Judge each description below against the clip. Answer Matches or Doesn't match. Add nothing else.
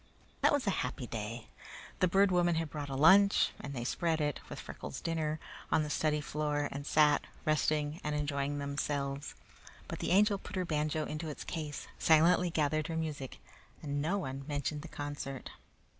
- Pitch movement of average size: Doesn't match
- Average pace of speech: Matches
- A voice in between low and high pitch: Matches